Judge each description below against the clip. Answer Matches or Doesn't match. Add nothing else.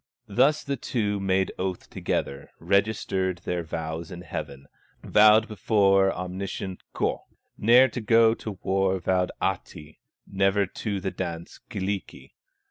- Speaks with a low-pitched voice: Matches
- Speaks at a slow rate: Matches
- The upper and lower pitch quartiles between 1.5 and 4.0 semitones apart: Matches